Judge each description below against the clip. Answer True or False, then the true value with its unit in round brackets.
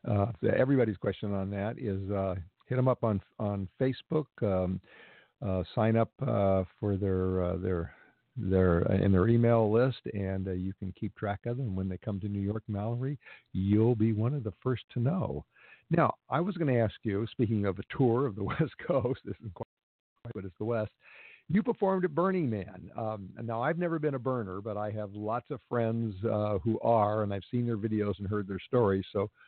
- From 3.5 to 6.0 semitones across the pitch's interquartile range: True (3.8 semitones)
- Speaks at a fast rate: True (215 wpm)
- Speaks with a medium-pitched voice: False (110 Hz)